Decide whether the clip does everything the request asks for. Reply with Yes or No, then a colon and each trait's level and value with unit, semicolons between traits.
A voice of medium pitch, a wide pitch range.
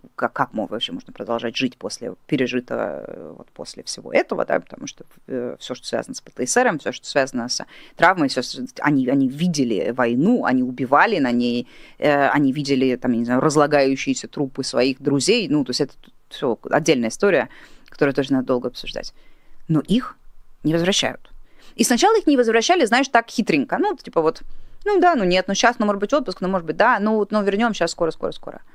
Yes: medium, 150 Hz; wide, 8.3 semitones